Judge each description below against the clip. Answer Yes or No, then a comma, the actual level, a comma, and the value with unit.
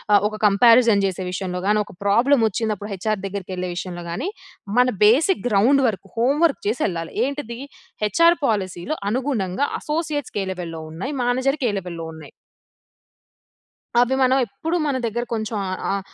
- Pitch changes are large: Yes, wide, 5.7 semitones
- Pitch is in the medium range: No, high, 215 Hz